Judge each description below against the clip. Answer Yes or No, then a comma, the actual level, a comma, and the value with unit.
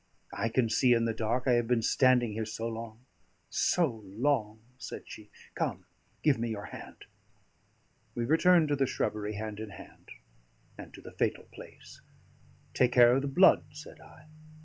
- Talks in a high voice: No, low, 120 Hz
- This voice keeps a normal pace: Yes, average, 170 wpm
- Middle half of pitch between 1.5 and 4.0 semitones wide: Yes, average, 3.2 semitones